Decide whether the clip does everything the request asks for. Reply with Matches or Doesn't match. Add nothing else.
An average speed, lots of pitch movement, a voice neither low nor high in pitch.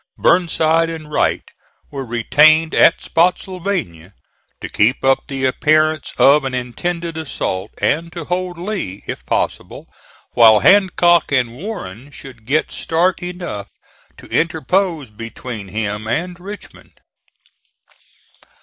Doesn't match